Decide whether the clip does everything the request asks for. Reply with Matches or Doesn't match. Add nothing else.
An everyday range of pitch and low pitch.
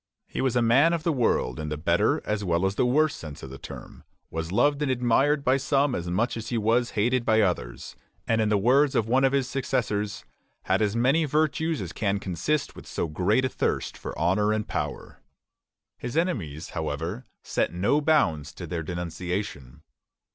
Doesn't match